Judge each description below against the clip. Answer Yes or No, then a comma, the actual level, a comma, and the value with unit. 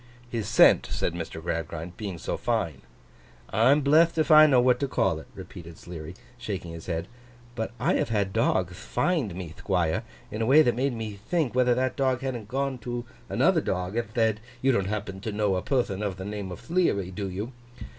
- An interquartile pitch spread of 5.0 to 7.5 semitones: Yes, wide, 5.5 semitones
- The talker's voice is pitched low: Yes, low, 110 Hz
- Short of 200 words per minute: No, fast, 205 wpm